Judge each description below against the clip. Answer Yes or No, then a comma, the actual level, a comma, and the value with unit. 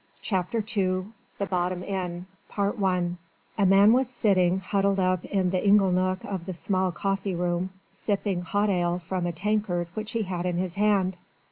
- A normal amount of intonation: No, narrow, 2.1 semitones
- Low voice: No, high, 190 Hz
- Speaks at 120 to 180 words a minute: Yes, average, 170 wpm